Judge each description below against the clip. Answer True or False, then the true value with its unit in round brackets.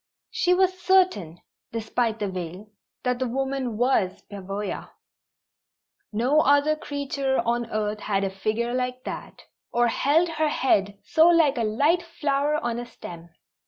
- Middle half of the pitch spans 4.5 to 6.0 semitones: True (5.6 semitones)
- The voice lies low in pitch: False (245 Hz)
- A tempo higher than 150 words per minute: False (145 wpm)